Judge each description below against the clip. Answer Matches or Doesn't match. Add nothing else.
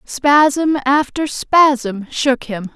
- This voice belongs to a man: Doesn't match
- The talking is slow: Matches